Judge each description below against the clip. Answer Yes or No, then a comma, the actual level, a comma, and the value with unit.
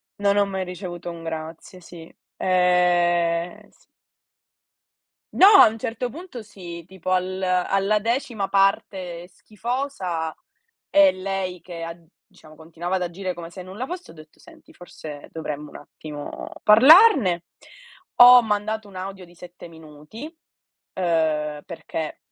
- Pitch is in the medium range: Yes, medium, 180 Hz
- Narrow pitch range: No, average, 3.5 semitones